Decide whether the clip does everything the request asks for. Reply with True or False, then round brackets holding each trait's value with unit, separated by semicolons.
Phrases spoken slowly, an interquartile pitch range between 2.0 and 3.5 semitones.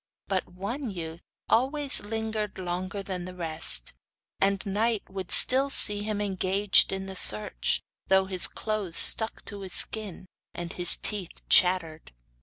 False (145 wpm; 2.8 semitones)